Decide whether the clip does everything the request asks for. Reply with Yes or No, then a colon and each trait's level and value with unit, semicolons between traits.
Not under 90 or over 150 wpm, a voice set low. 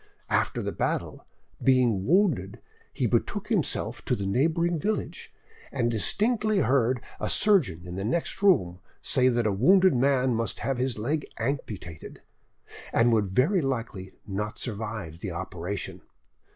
Yes: average, 140 wpm; low, 120 Hz